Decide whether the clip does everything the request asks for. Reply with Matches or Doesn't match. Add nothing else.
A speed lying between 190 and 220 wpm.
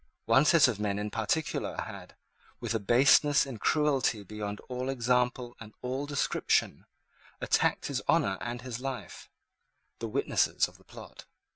Doesn't match